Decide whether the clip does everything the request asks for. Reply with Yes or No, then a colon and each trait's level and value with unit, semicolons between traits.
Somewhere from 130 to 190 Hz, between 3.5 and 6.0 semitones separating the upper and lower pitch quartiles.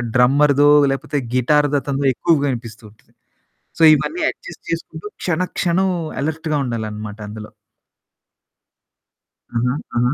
Yes: medium, 140 Hz; average, 4.9 semitones